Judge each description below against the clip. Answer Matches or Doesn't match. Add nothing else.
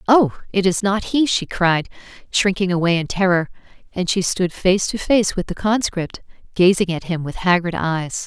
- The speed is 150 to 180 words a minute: Doesn't match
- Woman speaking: Matches